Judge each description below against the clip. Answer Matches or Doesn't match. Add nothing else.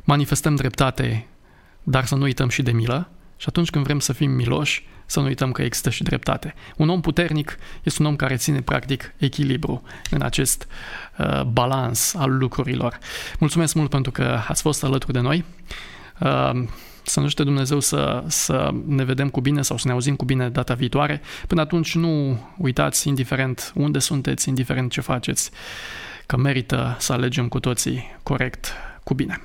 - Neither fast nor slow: Doesn't match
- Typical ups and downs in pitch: Doesn't match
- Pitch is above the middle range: Doesn't match